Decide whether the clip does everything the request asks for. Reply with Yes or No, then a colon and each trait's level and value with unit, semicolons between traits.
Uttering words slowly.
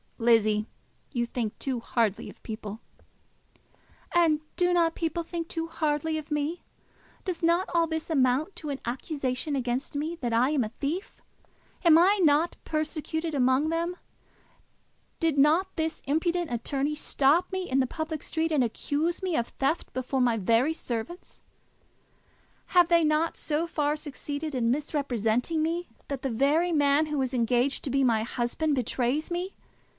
No: average, 160 wpm